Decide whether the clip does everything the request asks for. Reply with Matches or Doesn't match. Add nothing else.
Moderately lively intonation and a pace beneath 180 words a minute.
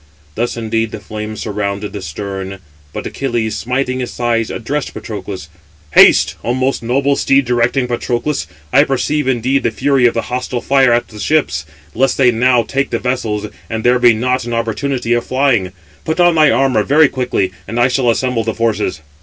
Doesn't match